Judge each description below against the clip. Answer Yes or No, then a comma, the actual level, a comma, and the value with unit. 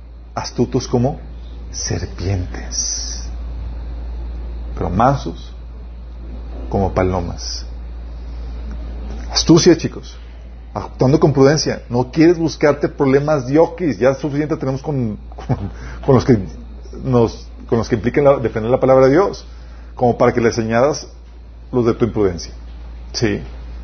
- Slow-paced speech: Yes, slow, 115 wpm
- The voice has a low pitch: Yes, very low, 80 Hz